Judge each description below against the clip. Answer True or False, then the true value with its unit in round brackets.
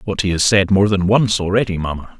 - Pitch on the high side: False (95 Hz)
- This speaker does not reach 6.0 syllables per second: True (5.8 syllables/s)